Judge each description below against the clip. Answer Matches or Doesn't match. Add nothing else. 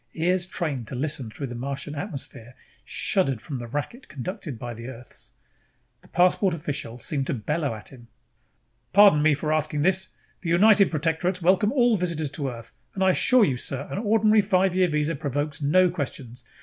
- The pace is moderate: Matches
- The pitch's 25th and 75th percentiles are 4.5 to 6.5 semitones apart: Matches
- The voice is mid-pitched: Matches